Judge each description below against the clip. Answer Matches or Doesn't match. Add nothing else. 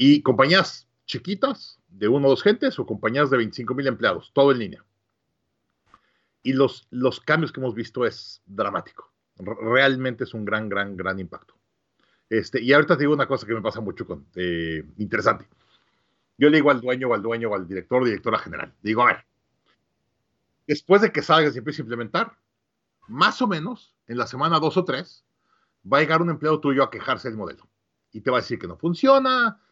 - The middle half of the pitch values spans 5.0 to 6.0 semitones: Matches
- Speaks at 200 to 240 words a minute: Matches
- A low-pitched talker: Matches